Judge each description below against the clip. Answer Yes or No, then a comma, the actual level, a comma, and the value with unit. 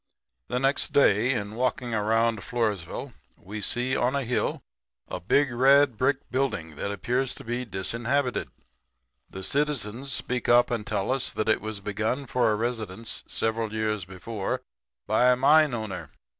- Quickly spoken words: No, average, 155 wpm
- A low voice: Yes, low, 115 Hz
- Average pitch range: Yes, average, 3.2 semitones